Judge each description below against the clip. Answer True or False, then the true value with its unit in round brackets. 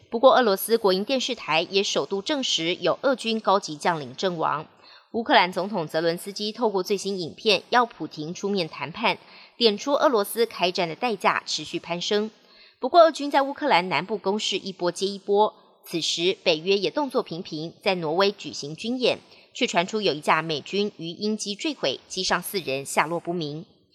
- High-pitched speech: True (195 Hz)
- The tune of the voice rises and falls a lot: False (4.7 semitones)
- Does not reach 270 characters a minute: False (285 characters per minute)